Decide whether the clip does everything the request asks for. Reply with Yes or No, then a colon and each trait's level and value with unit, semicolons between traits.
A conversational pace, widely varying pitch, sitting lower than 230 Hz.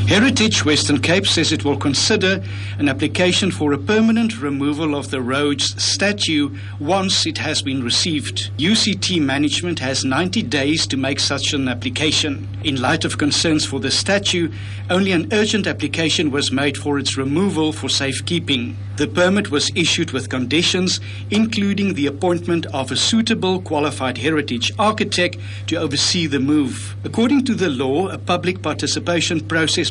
Yes: average, 155 wpm; wide, 7.3 semitones; medium, 140 Hz